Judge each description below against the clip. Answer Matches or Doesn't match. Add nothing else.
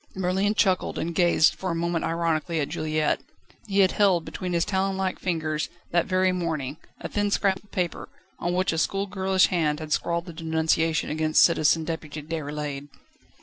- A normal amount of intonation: Matches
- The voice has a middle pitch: Matches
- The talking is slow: Doesn't match